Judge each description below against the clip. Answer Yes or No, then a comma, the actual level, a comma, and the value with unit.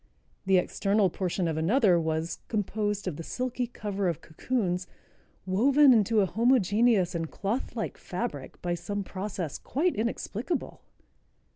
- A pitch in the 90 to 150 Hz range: No, high, 200 Hz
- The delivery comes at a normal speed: No, slow, 130 wpm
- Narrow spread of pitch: No, average, 4.5 semitones